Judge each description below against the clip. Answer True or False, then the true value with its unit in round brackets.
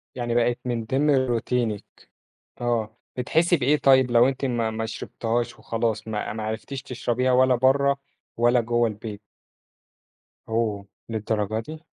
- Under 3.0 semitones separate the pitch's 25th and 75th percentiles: True (2.6 semitones)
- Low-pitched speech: True (120 Hz)